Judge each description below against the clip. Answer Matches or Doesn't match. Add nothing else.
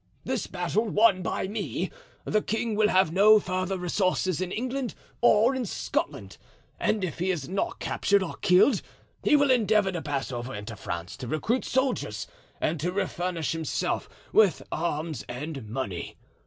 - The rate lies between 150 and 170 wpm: Matches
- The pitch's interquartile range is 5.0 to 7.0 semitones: Matches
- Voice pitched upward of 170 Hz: Matches